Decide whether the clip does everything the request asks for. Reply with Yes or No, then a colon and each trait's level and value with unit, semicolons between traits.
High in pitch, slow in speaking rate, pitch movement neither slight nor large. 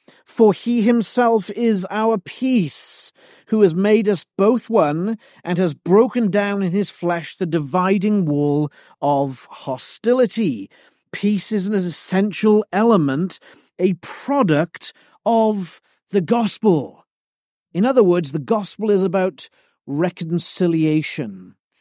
Yes: high, 200 Hz; slow, 115 wpm; average, 4.2 semitones